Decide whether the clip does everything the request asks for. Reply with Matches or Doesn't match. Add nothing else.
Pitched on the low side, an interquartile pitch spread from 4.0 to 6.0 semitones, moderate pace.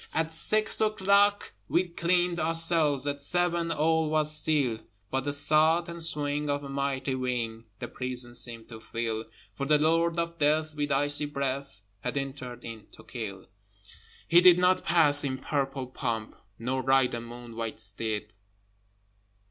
Doesn't match